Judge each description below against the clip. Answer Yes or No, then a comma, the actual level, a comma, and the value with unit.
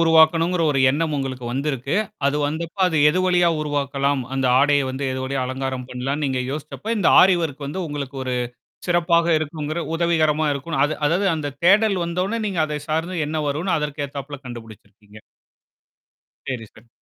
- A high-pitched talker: No, medium, 150 Hz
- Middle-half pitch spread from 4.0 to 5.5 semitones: No, average, 3.6 semitones